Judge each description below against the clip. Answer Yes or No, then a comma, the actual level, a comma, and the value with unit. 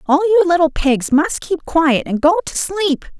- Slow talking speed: No, fast, 205 wpm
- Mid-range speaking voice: No, very high, 325 Hz